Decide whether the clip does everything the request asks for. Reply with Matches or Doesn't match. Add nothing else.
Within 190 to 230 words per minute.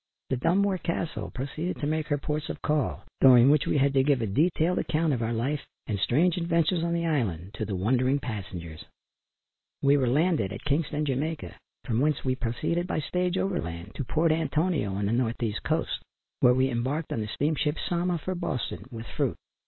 Matches